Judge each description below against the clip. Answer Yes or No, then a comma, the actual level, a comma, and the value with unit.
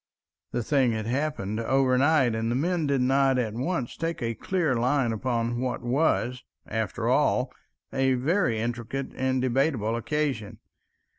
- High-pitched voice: No, low, 130 Hz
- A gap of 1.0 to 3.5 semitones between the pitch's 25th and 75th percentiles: Yes, average, 3.1 semitones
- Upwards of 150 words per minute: No, average, 145 wpm